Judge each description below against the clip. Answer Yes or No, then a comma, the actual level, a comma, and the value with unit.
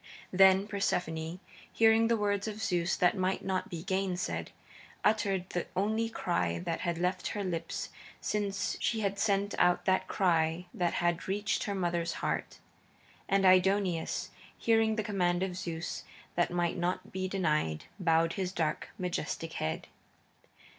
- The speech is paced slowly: No, average, 145 wpm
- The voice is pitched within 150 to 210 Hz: Yes, medium, 185 Hz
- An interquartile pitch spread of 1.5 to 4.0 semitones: Yes, narrow, 2.5 semitones